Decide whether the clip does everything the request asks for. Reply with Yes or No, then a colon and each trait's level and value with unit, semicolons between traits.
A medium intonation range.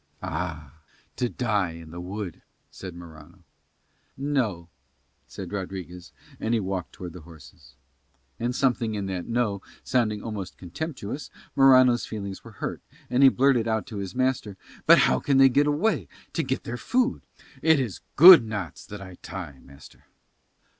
No: wide, 6.3 semitones